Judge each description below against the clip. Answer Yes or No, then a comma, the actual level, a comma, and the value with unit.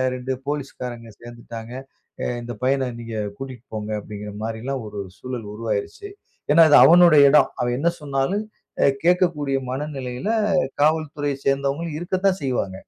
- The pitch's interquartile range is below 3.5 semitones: No, average, 4.1 semitones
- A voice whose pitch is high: No, low, 135 Hz